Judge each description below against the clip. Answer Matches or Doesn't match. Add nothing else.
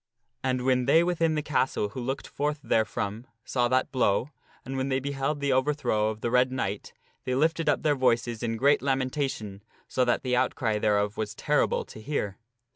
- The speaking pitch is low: Matches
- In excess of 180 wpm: Matches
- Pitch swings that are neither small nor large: Matches